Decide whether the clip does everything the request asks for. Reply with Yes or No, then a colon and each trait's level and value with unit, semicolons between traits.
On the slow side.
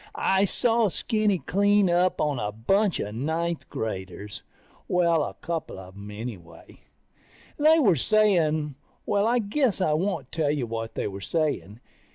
No: average, 155 wpm